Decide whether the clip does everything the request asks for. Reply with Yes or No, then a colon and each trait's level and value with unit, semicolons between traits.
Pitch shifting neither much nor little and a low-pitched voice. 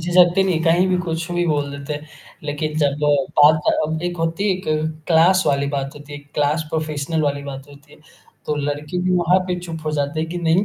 No: average, 3.1 semitones; medium, 155 Hz